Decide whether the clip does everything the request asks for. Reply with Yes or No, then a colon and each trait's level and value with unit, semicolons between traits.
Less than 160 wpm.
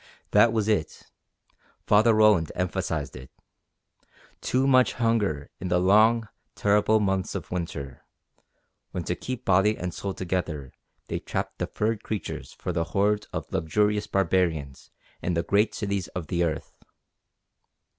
Yes: average, 140 wpm